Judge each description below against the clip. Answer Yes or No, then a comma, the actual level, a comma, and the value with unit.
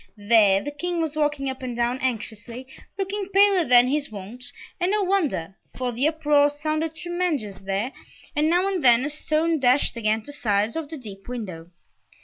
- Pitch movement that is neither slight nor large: No, wide, 5.7 semitones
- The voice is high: Yes, very high, 275 Hz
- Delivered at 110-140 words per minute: No, average, 180 wpm